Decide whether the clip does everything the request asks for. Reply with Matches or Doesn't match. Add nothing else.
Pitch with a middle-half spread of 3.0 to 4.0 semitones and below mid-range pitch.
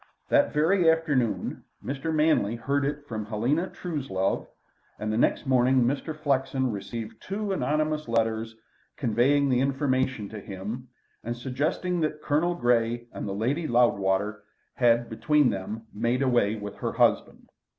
Doesn't match